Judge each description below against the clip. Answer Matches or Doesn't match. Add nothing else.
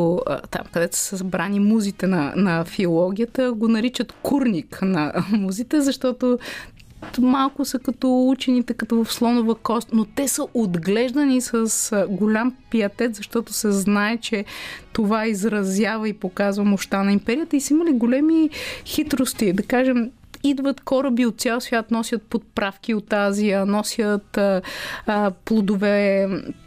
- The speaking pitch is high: Matches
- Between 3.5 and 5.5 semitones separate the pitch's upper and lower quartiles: Matches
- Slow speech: Doesn't match